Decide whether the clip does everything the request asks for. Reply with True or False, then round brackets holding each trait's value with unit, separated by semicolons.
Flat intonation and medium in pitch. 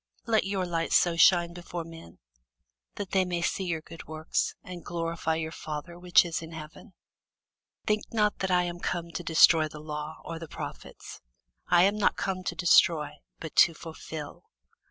True (2.0 semitones; 170 Hz)